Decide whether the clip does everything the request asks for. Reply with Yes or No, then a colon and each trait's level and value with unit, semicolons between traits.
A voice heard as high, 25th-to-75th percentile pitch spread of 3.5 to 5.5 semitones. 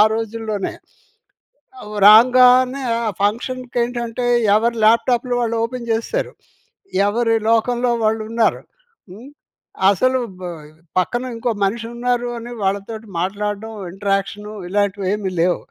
No: high, 230 Hz; average, 2.9 semitones